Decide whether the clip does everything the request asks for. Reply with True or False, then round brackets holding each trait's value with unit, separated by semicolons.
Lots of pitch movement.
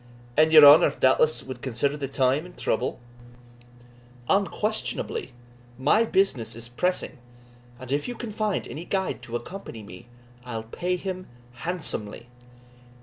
True (7.0 semitones)